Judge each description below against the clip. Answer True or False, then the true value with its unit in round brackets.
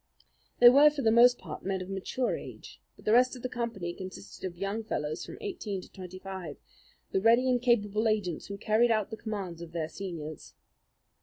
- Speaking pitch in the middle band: False (205 Hz)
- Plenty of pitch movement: False (4.4 semitones)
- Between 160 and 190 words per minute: False (205 wpm)